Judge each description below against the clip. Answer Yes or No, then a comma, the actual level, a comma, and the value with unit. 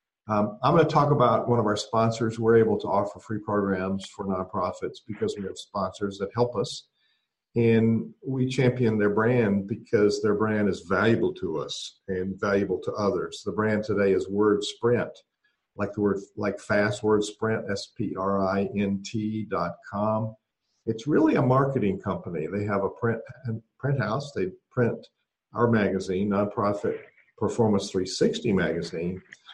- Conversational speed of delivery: Yes, average, 165 wpm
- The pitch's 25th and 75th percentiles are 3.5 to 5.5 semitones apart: No, average, 2.7 semitones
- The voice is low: Yes, low, 105 Hz